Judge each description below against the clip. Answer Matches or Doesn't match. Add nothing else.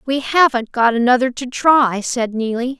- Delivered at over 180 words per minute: Doesn't match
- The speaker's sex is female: Matches